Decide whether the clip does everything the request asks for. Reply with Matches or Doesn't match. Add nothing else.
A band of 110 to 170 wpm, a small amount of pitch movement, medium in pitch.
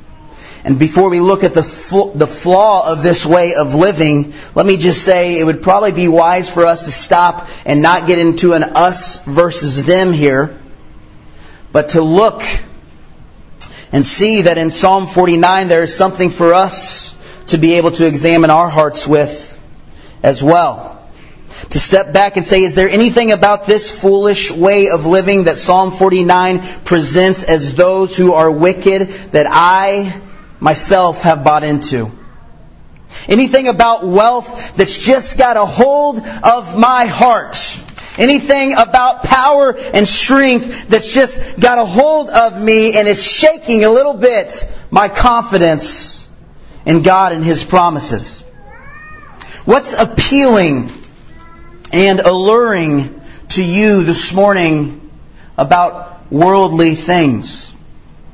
Doesn't match